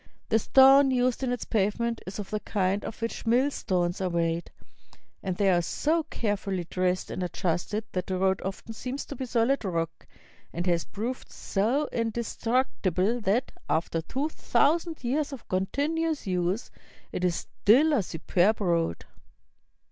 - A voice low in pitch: No, high, 210 Hz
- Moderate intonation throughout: No, wide, 5.8 semitones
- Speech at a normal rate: Yes, average, 155 wpm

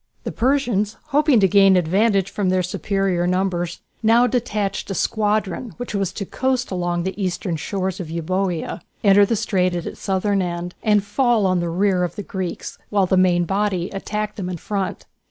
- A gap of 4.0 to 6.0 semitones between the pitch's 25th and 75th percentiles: No, narrow, 2.6 semitones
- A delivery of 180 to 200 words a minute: Yes, average, 190 wpm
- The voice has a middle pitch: No, high, 195 Hz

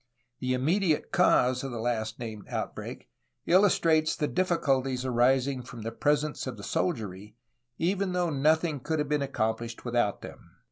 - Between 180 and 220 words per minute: No, average, 155 wpm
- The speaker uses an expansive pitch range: No, average, 5.0 semitones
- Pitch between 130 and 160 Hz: Yes, low, 135 Hz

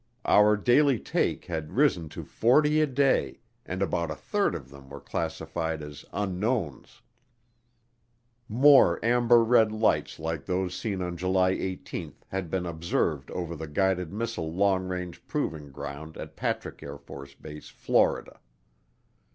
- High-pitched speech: No, very low, 90 Hz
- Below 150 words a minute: Yes, slow, 135 wpm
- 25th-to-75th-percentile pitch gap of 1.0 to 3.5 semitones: No, wide, 5.4 semitones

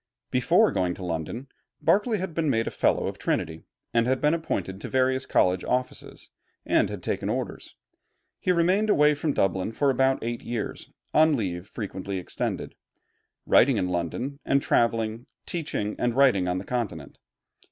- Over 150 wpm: Yes, average, 160 wpm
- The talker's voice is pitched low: Yes, low, 120 Hz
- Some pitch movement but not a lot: No, wide, 7.0 semitones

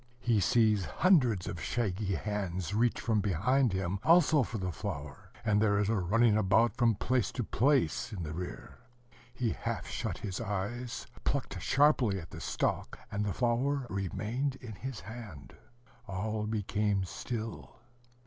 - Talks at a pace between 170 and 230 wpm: No, average, 155 wpm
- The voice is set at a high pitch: No, low, 110 Hz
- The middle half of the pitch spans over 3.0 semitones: Yes, average, 3.8 semitones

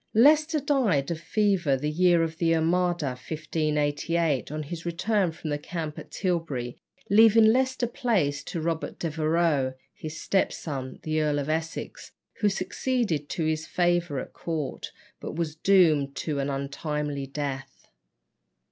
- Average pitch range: Yes, average, 3.6 semitones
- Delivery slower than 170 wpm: Yes, average, 145 wpm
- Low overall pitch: No, medium, 160 Hz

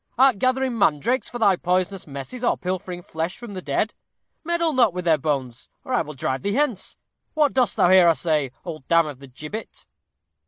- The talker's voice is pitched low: No, medium, 185 Hz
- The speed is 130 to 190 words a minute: No, average, 200 wpm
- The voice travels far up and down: Yes, wide, 8.0 semitones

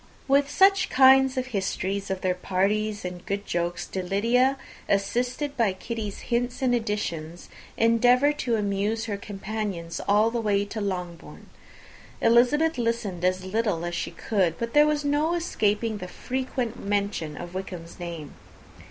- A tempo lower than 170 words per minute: Yes, average, 150 wpm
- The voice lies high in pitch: Yes, high, 210 Hz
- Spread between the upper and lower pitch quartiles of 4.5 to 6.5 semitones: Yes, average, 4.8 semitones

